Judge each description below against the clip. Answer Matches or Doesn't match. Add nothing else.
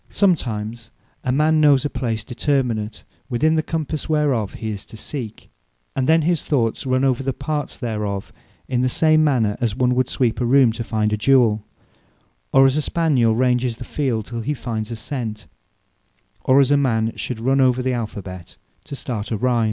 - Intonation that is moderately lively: Matches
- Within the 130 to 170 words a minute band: Doesn't match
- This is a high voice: Doesn't match